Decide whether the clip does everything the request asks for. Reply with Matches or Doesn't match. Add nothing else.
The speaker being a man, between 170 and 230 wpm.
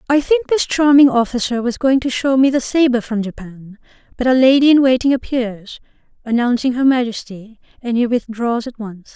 Doesn't match